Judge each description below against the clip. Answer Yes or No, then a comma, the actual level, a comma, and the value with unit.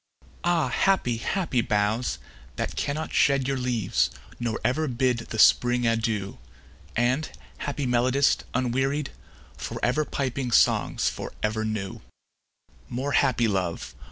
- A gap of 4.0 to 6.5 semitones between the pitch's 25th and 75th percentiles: No, average, 3.5 semitones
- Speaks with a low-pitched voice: Yes, low, 125 Hz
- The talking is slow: Yes, slow, 125 wpm